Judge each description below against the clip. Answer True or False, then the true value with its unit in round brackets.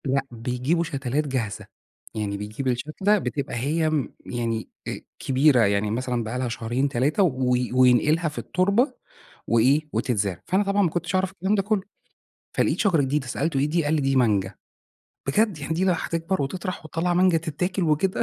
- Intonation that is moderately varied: False (6.0 semitones)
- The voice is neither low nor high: True (145 Hz)